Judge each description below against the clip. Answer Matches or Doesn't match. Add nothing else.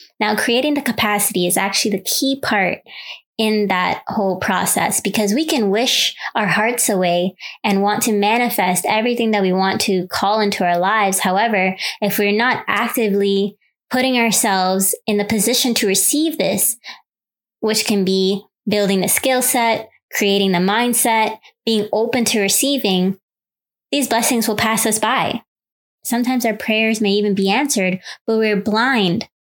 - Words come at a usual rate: Matches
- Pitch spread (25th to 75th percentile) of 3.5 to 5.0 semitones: Doesn't match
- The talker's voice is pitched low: Doesn't match